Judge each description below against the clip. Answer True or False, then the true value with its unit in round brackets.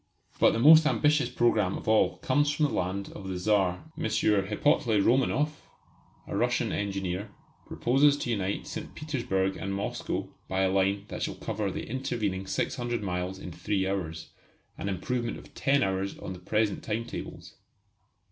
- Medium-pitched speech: False (105 Hz)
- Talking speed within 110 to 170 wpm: True (165 wpm)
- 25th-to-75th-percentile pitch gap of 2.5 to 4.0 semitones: False (4.8 semitones)